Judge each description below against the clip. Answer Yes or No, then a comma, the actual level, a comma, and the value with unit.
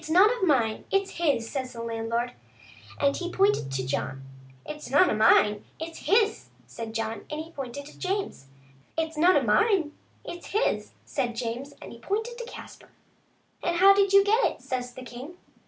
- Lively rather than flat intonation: Yes, wide, 8.6 semitones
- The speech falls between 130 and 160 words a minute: No, average, 200 wpm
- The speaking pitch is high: Yes, very high, 285 Hz